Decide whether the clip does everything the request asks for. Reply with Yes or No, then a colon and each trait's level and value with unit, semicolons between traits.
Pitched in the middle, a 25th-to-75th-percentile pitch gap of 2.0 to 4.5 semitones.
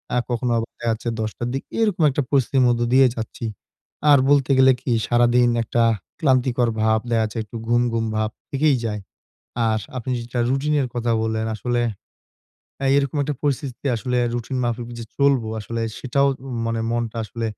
No: low, 120 Hz; average, 2.8 semitones